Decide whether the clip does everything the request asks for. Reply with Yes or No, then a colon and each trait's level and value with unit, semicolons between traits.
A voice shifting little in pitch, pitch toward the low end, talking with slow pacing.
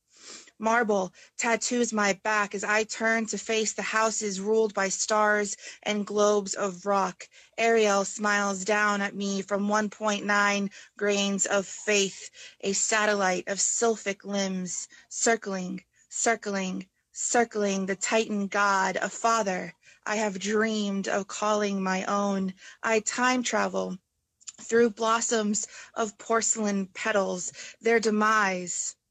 No: narrow, 2.1 semitones; high, 205 Hz; slow, 120 wpm